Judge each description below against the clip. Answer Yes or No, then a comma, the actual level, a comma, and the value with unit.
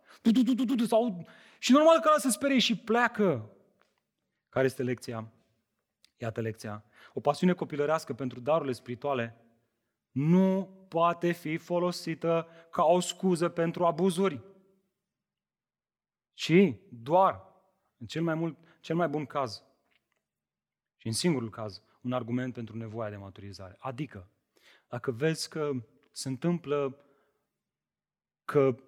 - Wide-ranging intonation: Yes, wide, 7.3 semitones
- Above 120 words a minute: No, slow, 115 wpm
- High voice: No, medium, 150 Hz